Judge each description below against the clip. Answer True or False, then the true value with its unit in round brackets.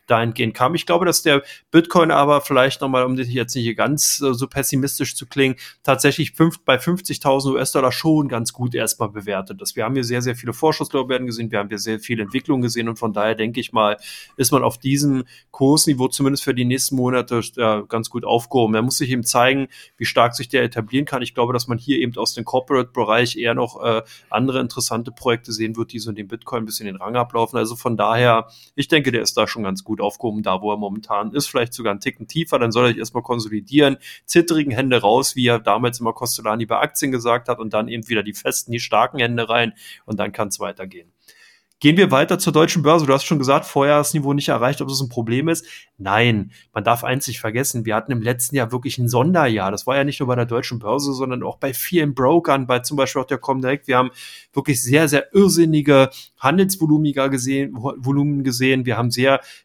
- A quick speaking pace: True (225 wpm)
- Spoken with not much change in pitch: False (3.3 semitones)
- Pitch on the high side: False (125 Hz)